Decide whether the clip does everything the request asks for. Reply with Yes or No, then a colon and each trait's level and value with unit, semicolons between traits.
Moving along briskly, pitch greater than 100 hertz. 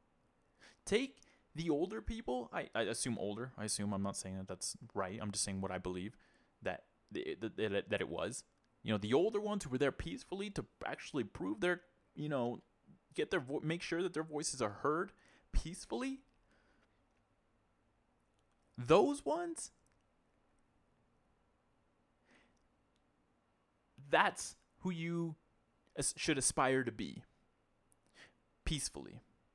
No: slow, 135 wpm; low, 135 Hz